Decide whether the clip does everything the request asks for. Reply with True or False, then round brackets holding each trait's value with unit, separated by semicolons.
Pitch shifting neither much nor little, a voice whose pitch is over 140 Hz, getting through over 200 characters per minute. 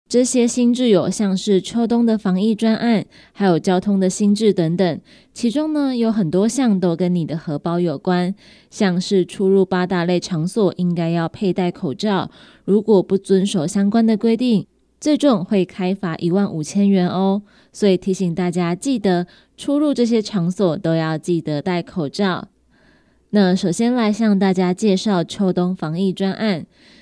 True (3.3 semitones; 190 Hz; 245 characters per minute)